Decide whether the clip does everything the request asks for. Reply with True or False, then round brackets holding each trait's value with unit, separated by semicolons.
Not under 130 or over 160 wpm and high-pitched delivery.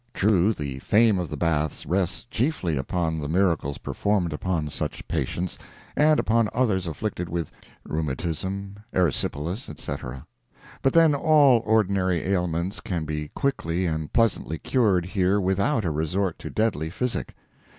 False (140 wpm; 90 Hz)